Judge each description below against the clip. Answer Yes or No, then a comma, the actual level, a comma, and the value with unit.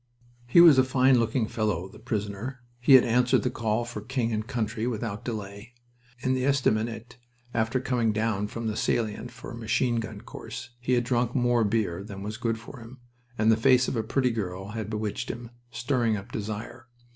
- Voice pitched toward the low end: Yes, low, 115 Hz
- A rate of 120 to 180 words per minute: No, average, 195 wpm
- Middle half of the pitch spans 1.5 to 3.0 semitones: Yes, narrow, 2.4 semitones